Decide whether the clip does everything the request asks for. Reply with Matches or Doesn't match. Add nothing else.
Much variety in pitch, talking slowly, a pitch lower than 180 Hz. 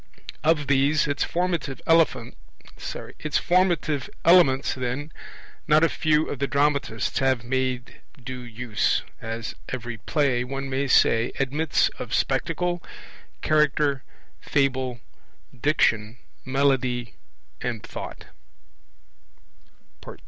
Doesn't match